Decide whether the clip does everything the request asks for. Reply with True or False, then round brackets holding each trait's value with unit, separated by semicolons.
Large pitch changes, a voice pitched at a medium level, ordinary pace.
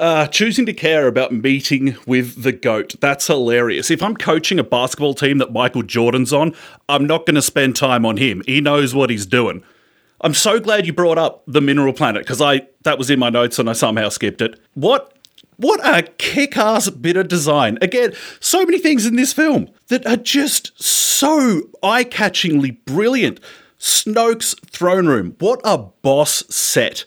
True (8.4 semitones; 155 Hz; 180 wpm)